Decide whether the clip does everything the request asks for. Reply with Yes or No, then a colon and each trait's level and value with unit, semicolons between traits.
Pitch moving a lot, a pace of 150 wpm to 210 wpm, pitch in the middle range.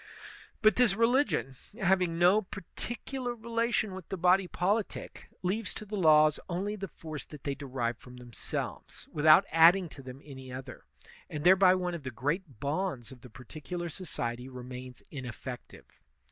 Yes: wide, 6.6 semitones; average, 160 wpm; medium, 165 Hz